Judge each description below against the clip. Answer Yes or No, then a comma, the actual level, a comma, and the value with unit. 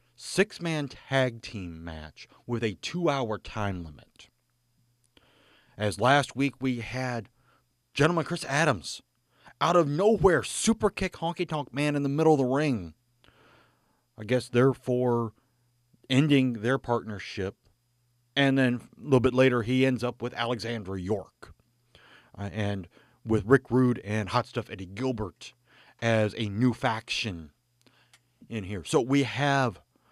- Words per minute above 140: No, slow, 135 wpm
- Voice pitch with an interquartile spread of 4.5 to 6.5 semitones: No, average, 3.9 semitones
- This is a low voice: Yes, low, 120 Hz